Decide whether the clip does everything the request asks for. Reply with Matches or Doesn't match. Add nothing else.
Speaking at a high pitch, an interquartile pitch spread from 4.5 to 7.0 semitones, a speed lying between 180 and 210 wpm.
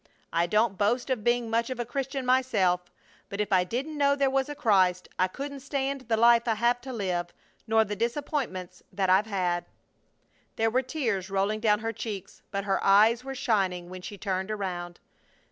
Matches